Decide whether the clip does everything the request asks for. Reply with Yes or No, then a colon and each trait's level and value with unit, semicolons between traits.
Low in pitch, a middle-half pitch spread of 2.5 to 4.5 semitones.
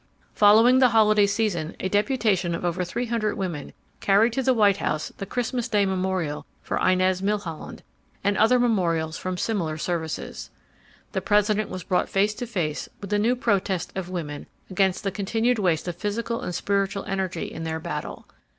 No: high, 195 Hz; average, 3.5 semitones